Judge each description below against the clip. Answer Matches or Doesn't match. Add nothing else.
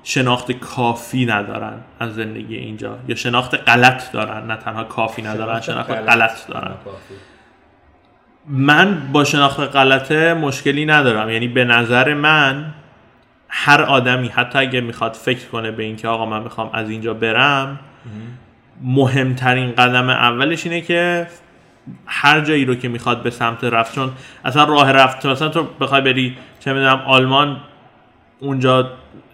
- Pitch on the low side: Matches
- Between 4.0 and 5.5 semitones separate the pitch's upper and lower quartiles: Doesn't match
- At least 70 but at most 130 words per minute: Doesn't match